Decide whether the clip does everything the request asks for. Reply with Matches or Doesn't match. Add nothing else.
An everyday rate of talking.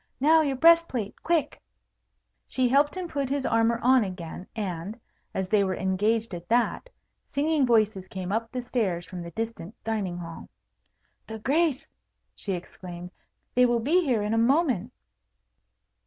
Matches